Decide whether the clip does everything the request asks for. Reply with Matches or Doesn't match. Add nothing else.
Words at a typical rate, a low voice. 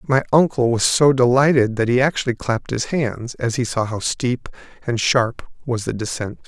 Matches